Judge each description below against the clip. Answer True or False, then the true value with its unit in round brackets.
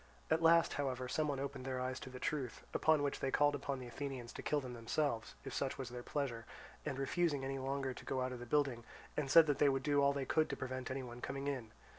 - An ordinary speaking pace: False (250 wpm)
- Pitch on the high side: False (135 Hz)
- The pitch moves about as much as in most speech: False (2.0 semitones)